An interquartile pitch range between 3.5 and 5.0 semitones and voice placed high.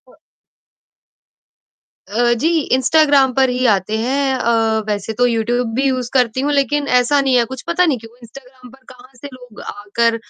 No: narrow, 2.5 semitones; very high, 250 Hz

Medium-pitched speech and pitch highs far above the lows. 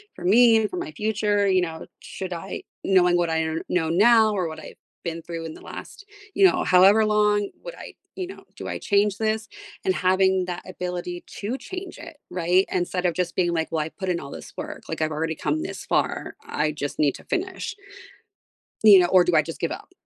No: medium, 180 Hz; average, 3.9 semitones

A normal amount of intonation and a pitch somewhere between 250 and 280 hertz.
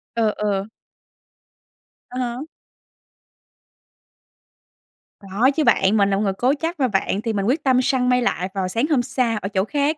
No: average, 4.6 semitones; high, 235 Hz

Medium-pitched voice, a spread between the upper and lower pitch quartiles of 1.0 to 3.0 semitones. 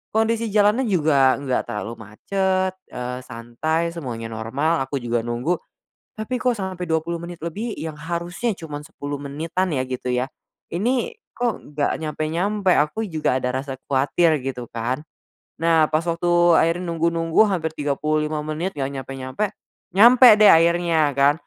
No: medium, 160 Hz; average, 4.9 semitones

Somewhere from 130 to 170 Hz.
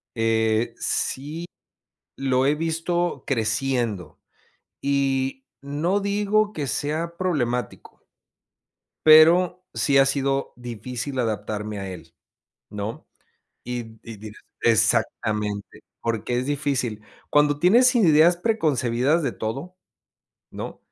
Yes: low, 135 Hz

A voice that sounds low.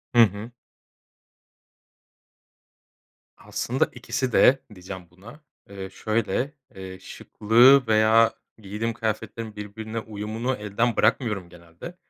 Yes: low, 110 Hz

